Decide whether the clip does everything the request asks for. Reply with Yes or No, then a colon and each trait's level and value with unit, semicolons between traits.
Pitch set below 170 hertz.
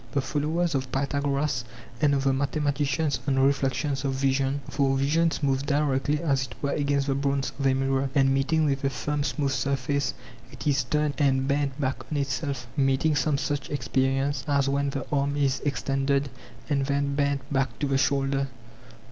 Yes: medium, 140 Hz